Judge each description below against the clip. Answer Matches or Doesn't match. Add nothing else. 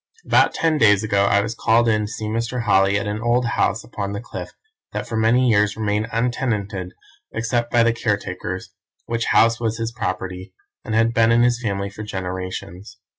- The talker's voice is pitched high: Doesn't match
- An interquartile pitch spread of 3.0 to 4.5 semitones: Doesn't match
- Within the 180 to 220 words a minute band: Matches